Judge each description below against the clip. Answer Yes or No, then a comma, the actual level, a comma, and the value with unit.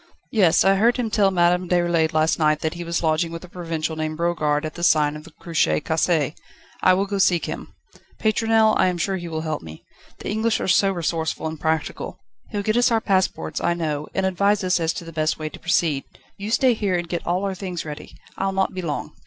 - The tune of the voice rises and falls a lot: No, average, 3.4 semitones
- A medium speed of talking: No, fast, 235 wpm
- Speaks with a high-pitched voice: No, medium, 175 Hz